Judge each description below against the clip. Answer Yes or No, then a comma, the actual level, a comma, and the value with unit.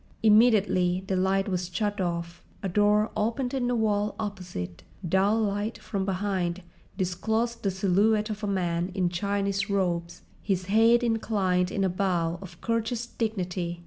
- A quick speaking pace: No, average, 150 wpm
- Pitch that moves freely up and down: No, average, 3.0 semitones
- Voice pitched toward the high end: Yes, high, 195 Hz